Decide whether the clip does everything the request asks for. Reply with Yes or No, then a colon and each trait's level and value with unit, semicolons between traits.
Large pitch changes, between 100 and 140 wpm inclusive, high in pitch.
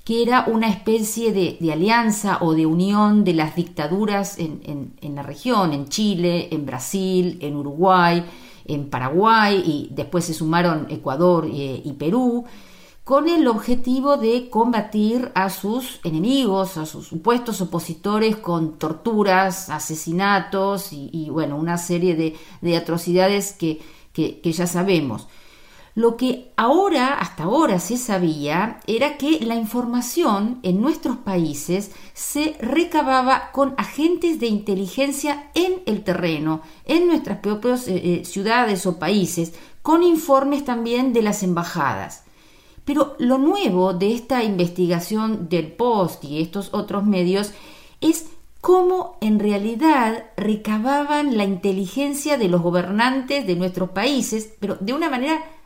Yes: wide, 6.1 semitones; average, 135 wpm; high, 200 Hz